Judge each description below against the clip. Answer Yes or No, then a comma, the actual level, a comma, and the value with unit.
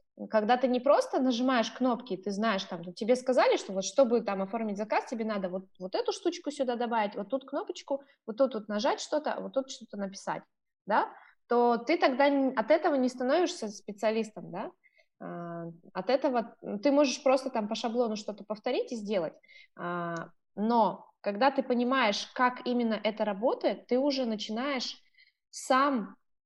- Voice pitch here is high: Yes, high, 245 Hz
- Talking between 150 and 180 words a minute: Yes, fast, 160 wpm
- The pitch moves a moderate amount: Yes, average, 4.6 semitones